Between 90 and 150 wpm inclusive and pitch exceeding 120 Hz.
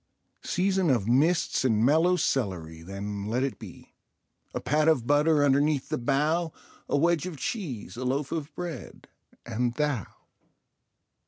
Yes: average, 140 wpm; medium, 140 Hz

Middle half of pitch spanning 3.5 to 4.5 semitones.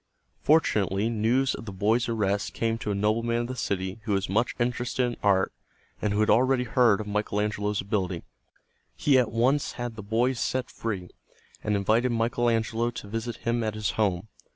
No: average, 2.7 semitones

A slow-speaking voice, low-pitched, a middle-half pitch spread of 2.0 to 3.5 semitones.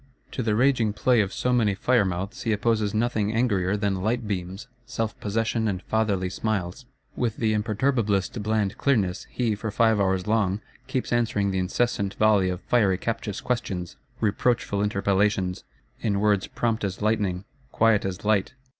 No: average, 160 wpm; low, 105 Hz; narrow, 2.6 semitones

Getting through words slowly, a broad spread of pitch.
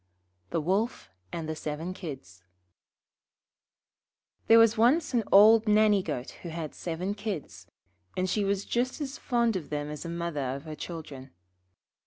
No: average, 155 wpm; wide, 6.2 semitones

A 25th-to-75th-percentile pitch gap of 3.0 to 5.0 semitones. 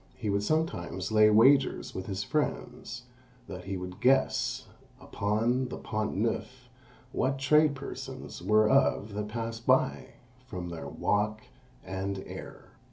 Yes: average, 4.1 semitones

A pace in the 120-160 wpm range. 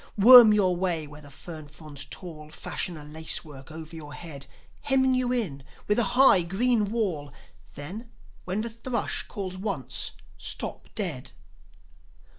Yes: average, 150 wpm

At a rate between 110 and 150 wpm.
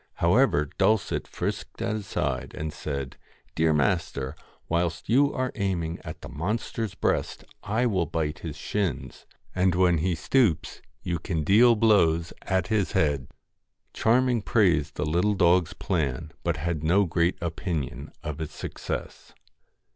Yes: average, 145 wpm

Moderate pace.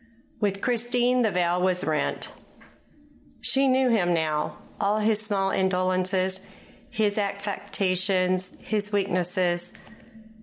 No: slow, 105 wpm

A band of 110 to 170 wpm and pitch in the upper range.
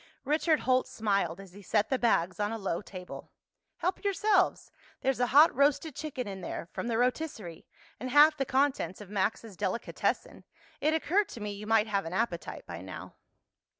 No: average, 185 wpm; high, 230 Hz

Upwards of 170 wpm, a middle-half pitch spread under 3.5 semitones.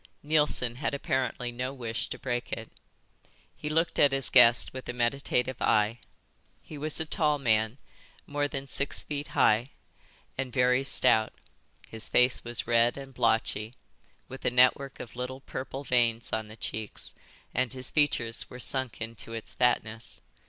No: average, 160 wpm; average, 2.8 semitones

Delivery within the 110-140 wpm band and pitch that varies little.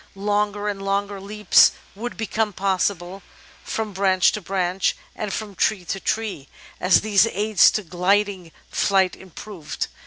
Yes: slow, 135 wpm; narrow, 1.9 semitones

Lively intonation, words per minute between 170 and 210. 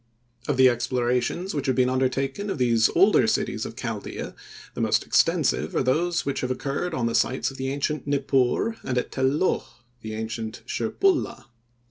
No: average, 2.8 semitones; average, 175 wpm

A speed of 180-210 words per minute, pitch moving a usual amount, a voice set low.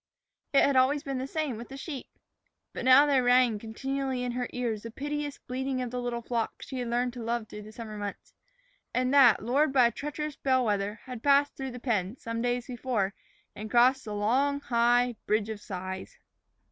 No: fast, 205 wpm; average, 3.0 semitones; high, 245 Hz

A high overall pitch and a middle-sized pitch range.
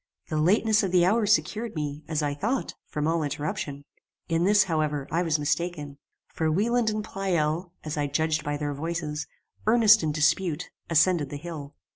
No: medium, 160 Hz; average, 4.4 semitones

